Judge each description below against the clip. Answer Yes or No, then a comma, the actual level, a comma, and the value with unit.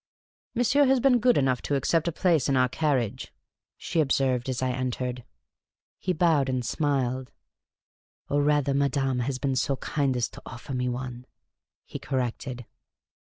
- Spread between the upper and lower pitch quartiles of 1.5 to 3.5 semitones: Yes, average, 2.9 semitones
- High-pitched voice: No, low, 135 Hz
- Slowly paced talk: No, average, 165 wpm